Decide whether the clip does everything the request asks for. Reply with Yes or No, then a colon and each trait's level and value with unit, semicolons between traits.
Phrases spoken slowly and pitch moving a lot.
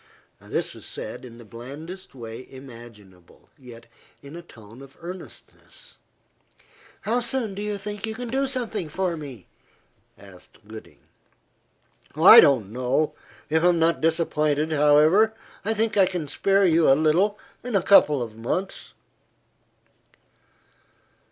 Yes: slow, 130 wpm; wide, 7.8 semitones